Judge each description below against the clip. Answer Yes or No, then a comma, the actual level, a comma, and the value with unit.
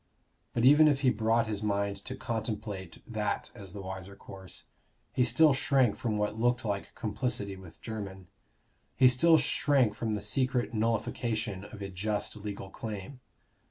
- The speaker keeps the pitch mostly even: No, average, 3.6 semitones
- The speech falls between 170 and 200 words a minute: No, average, 160 wpm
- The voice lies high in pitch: No, low, 110 Hz